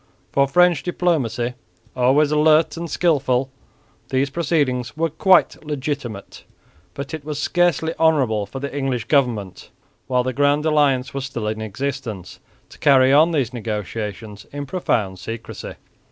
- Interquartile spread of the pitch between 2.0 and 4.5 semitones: Yes, average, 4.1 semitones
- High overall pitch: No, low, 135 Hz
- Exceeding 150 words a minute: No, average, 140 wpm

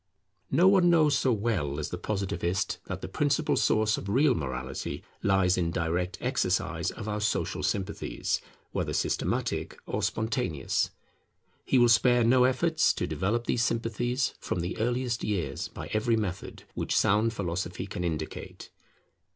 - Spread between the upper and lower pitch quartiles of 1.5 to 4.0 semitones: No, average, 5.1 semitones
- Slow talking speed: No, average, 150 wpm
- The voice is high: No, low, 105 Hz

